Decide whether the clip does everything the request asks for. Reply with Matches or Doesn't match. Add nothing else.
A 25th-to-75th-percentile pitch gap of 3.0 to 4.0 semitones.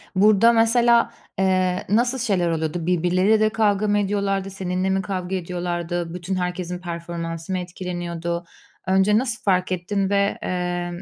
Doesn't match